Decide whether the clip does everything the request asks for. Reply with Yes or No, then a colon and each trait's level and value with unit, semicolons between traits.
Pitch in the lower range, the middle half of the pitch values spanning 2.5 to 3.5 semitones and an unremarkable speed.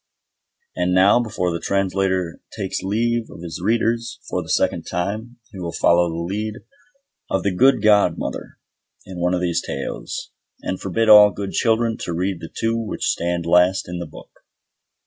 No: very low, 95 Hz; average, 3.9 semitones; average, 170 wpm